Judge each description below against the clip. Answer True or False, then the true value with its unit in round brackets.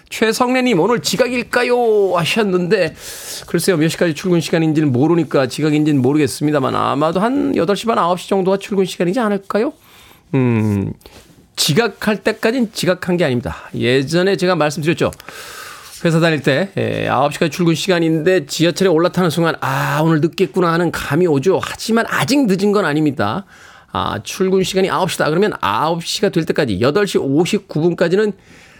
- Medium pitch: True (175 Hz)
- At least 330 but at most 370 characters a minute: True (340 characters per minute)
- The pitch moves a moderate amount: True (4.5 semitones)